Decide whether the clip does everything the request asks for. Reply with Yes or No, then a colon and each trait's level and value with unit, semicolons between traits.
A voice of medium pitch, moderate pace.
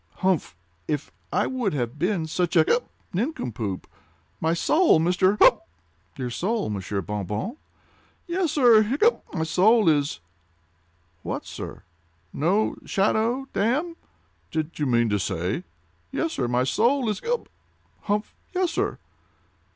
No: medium, 180 Hz; slow, 110 wpm